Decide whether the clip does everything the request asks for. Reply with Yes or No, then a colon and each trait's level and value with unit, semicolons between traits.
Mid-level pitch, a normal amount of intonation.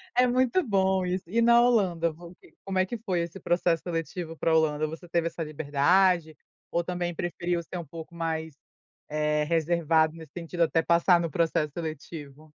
No: medium, 170 Hz; narrow, 2.3 semitones